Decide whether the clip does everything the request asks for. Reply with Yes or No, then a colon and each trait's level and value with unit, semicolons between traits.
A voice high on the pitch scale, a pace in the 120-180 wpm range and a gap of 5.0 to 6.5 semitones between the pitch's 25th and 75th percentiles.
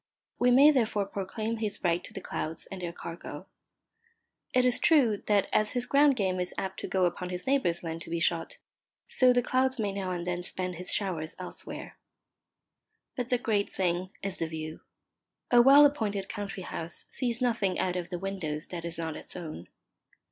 No: high, 195 Hz; average, 190 wpm; wide, 5.6 semitones